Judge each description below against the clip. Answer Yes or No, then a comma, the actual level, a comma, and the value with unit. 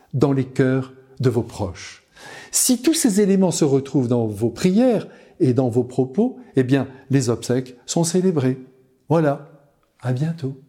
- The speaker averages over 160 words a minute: No, average, 155 wpm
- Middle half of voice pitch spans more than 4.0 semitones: Yes, average, 4.6 semitones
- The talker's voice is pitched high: No, low, 135 Hz